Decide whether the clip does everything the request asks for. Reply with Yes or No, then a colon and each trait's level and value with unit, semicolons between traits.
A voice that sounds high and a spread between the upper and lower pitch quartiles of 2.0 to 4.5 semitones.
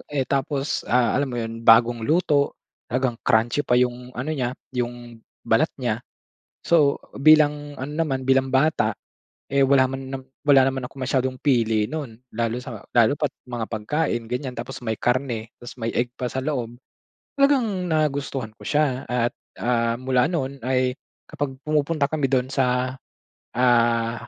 No: low, 130 Hz; average, 2.8 semitones